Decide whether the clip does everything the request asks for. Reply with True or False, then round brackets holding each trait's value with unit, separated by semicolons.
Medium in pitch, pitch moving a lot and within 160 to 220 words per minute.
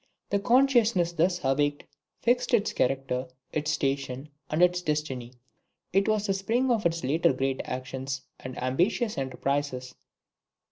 False (150 Hz; 6.8 semitones; 135 wpm)